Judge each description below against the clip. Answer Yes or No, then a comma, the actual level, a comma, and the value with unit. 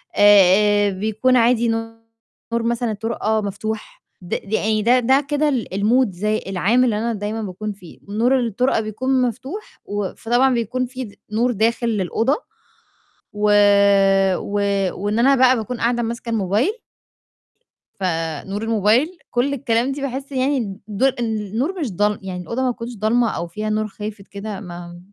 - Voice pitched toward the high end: Yes, high, 225 Hz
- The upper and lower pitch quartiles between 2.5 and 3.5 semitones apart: Yes, average, 3.2 semitones